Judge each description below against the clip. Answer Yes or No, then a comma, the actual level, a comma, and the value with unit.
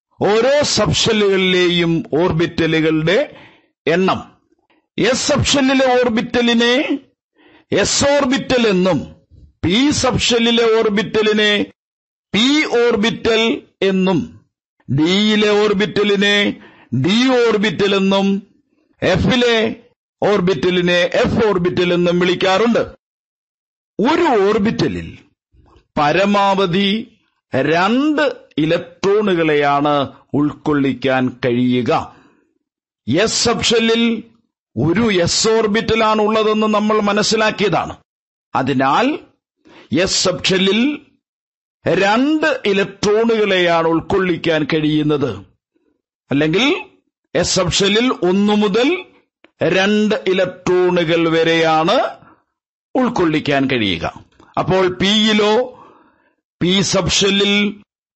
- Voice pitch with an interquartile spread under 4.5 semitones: No, average, 5.0 semitones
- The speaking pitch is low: No, high, 205 Hz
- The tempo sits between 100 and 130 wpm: No, average, 65 wpm